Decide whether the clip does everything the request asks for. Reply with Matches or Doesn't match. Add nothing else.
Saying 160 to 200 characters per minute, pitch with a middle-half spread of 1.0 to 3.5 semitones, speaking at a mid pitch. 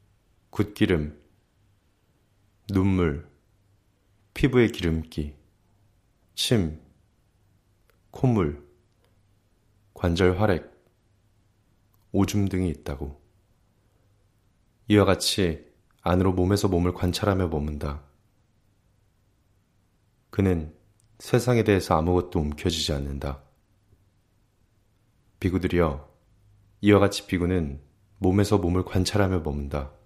Doesn't match